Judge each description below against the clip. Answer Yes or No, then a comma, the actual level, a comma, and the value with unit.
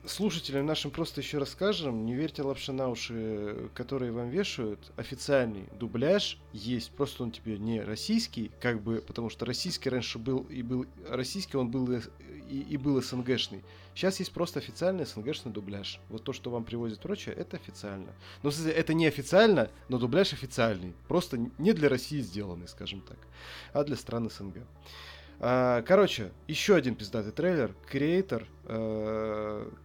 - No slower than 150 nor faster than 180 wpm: Yes, average, 155 wpm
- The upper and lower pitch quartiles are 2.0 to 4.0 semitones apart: No, average, 5.0 semitones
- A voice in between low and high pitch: No, low, 125 Hz